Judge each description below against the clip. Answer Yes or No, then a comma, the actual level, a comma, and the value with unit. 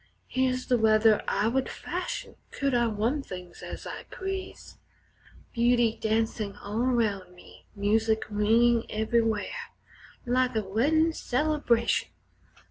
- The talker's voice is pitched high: Yes, high, 230 Hz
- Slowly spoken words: Yes, slow, 120 wpm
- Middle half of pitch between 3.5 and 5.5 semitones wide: No, average, 2.9 semitones